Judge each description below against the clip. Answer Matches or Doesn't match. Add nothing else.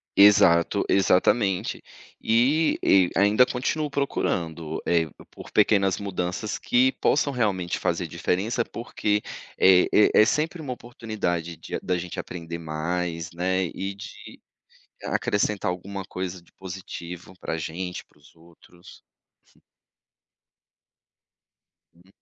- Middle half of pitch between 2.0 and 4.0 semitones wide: Matches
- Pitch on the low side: Matches